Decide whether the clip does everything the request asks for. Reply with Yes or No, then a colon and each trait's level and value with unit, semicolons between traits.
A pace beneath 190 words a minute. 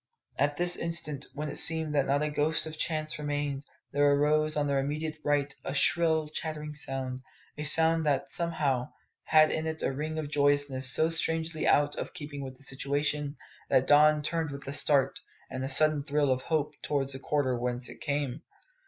No: average, 195 wpm